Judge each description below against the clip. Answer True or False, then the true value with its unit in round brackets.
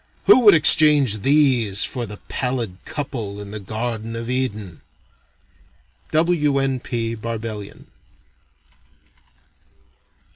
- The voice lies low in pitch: True (120 Hz)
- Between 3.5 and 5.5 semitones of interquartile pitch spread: True (4.4 semitones)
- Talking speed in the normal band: False (100 wpm)